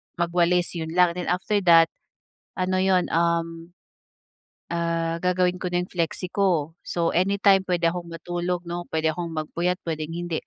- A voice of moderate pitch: Yes, medium, 175 Hz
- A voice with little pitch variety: Yes, narrow, 1.4 semitones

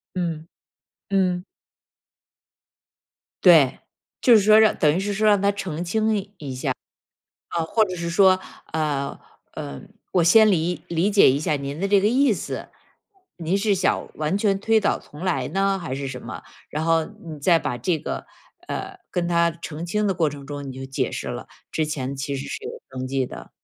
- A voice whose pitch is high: No, medium, 170 Hz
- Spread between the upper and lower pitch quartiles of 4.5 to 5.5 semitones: Yes, average, 5.1 semitones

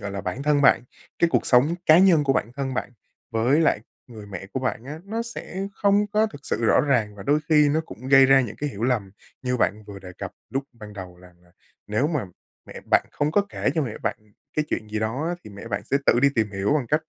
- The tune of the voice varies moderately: No, wide, 6.1 semitones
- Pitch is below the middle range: Yes, low, 130 Hz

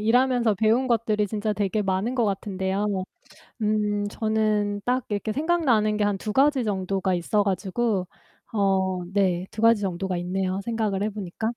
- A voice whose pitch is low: No, high, 210 Hz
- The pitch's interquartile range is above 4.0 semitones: No, narrow, 2.6 semitones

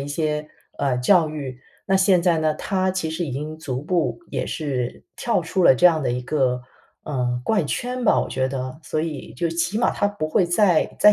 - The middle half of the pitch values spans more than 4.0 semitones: Yes, average, 5.2 semitones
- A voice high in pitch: No, medium, 155 Hz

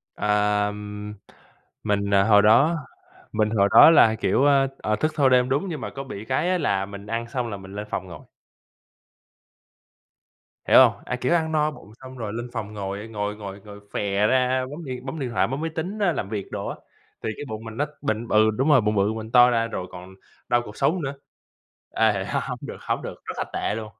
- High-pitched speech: No, low, 110 Hz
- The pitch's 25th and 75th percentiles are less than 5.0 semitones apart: Yes, average, 4.4 semitones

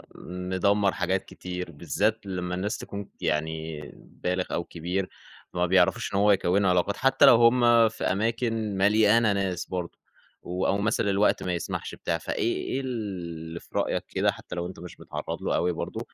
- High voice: No, very low, 95 Hz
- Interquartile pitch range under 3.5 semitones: Yes, average, 3.1 semitones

